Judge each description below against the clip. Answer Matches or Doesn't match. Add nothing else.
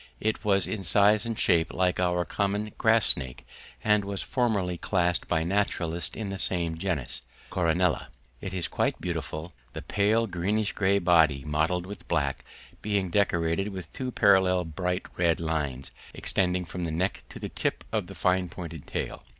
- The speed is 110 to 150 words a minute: Doesn't match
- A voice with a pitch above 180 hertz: Doesn't match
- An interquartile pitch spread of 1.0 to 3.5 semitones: Matches